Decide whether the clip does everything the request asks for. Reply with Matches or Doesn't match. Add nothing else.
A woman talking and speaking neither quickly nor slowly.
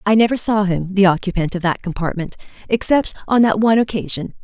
Matches